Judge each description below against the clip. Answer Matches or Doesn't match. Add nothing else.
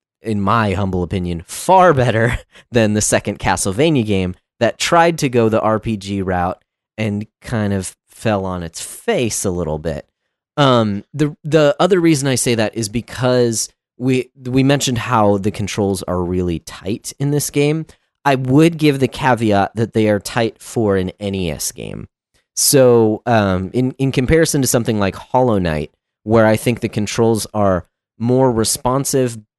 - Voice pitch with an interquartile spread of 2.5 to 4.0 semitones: Doesn't match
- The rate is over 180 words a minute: Doesn't match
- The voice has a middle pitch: Doesn't match